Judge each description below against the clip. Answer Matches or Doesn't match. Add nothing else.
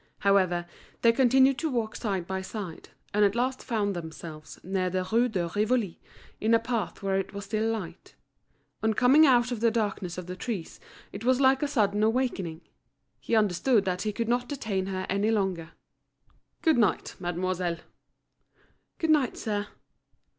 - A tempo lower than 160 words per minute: Doesn't match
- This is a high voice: Matches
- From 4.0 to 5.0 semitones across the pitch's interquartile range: Matches